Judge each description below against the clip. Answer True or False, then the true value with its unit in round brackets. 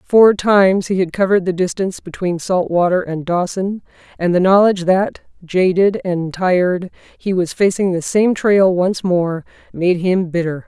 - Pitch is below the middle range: False (185 Hz)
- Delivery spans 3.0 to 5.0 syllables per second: True (4.6 syllables/s)